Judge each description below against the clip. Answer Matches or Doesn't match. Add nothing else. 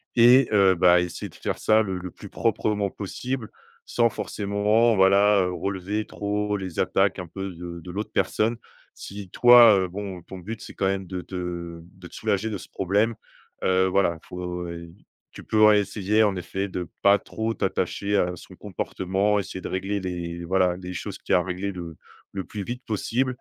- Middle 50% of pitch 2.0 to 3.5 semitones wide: Matches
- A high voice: Doesn't match